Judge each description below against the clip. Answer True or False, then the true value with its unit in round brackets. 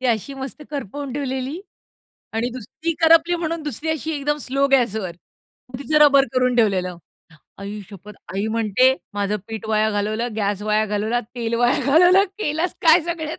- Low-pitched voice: False (255 Hz)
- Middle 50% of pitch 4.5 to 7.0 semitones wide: True (5.6 semitones)